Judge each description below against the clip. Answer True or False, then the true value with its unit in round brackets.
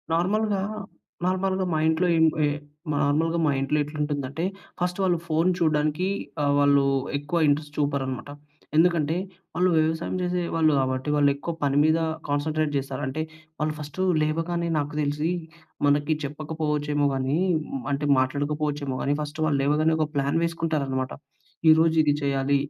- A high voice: False (150 Hz)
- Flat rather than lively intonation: True (2.2 semitones)